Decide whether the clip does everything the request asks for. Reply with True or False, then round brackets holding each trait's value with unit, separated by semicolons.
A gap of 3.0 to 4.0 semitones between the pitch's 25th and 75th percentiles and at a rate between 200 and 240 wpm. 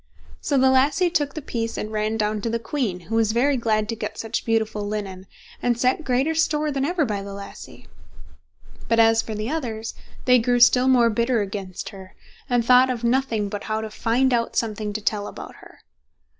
True (3.3 semitones; 205 wpm)